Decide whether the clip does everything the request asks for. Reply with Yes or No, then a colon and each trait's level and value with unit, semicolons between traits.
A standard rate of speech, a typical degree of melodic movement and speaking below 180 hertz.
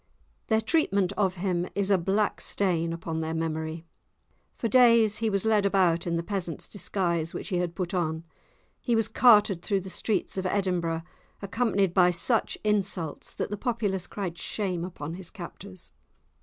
No: average, 170 wpm; average, 3.4 semitones; high, 190 Hz